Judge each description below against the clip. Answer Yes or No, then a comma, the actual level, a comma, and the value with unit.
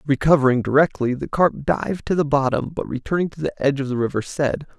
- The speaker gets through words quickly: Yes, fast, 215 wpm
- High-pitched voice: No, medium, 140 Hz